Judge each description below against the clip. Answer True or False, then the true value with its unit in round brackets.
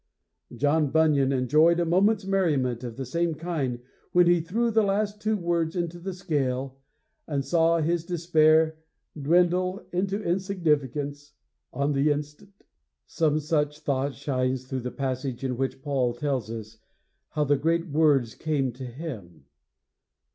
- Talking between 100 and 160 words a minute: True (150 wpm)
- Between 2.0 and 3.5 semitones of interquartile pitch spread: False (4.3 semitones)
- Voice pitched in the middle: True (150 Hz)